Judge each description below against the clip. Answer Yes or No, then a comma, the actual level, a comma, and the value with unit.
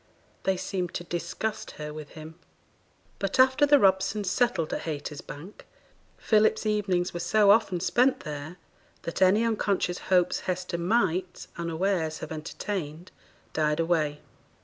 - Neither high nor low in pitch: Yes, medium, 180 Hz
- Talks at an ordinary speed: No, slow, 130 wpm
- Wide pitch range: No, average, 4.1 semitones